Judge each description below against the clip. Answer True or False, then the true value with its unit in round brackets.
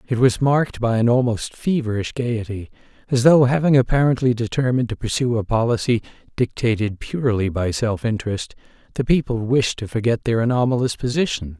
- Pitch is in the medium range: False (120 Hz)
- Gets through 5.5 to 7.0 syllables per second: True (5.7 syllables/s)